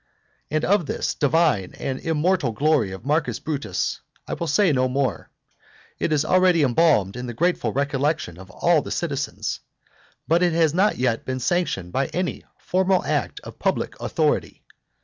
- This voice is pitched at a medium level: Yes, medium, 150 Hz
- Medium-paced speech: Yes, average, 165 wpm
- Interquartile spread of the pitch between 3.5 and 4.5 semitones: No, average, 5.2 semitones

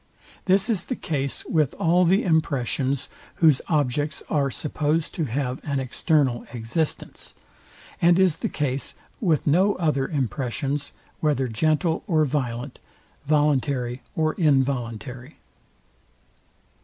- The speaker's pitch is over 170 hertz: No, medium, 145 Hz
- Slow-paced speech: Yes, slow, 115 wpm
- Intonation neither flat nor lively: Yes, average, 3.4 semitones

